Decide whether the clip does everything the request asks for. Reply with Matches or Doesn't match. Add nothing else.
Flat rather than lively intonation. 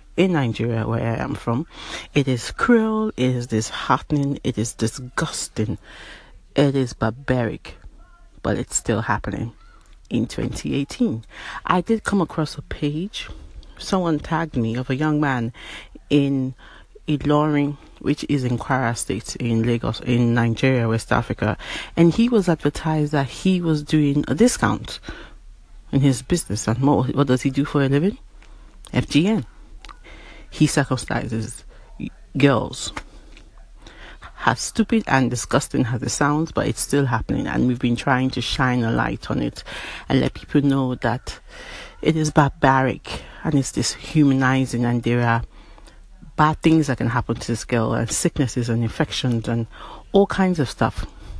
Doesn't match